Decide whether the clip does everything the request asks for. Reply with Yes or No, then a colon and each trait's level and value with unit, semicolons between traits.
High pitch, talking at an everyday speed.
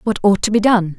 No: high, 205 Hz; fast, 305 wpm